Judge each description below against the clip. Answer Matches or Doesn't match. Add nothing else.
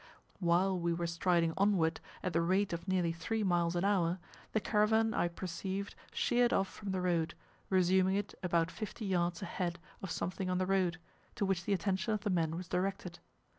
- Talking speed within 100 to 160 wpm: Doesn't match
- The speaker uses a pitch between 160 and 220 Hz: Matches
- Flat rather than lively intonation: Matches